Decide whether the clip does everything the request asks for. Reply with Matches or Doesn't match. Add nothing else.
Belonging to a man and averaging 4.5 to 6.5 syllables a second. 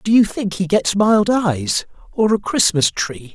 Doesn't match